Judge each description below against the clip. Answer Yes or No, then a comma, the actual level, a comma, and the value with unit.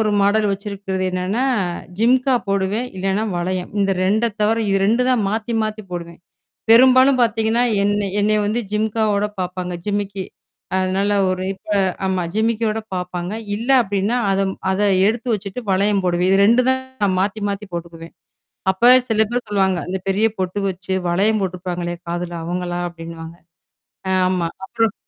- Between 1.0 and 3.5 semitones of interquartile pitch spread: Yes, average, 3.1 semitones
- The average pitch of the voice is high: Yes, high, 200 Hz